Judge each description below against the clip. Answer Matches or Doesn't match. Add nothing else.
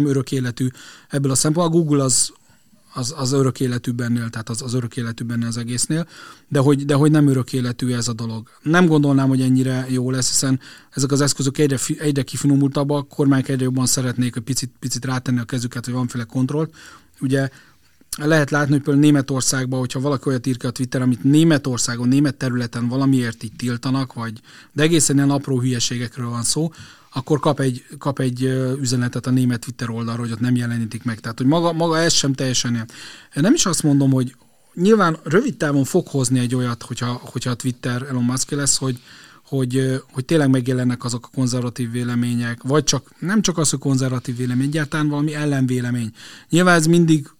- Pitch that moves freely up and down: Doesn't match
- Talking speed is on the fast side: Matches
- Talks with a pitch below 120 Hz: Doesn't match